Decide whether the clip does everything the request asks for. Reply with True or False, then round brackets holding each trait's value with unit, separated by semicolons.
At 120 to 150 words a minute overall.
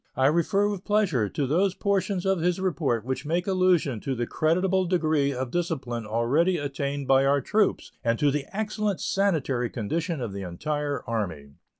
False (175 wpm)